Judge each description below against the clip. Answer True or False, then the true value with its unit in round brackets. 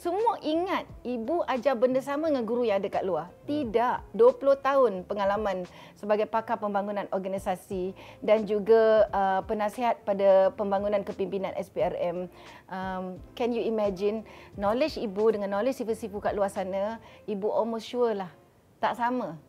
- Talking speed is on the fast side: False (140 wpm)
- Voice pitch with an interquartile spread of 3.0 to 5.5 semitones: True (3.8 semitones)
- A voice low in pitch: False (215 Hz)